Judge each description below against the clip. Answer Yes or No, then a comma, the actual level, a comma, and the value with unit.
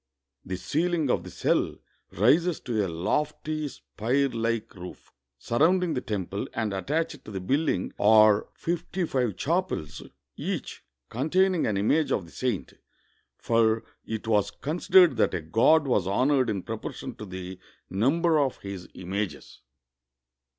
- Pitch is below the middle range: Yes, low, 115 Hz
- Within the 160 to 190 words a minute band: No, average, 145 wpm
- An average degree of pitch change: No, wide, 7.5 semitones